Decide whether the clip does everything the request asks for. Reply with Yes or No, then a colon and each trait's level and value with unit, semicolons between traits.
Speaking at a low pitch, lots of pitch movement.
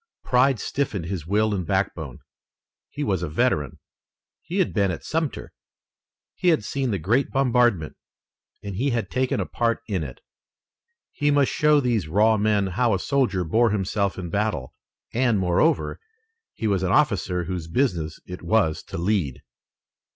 Yes: low, 105 Hz; wide, 5.7 semitones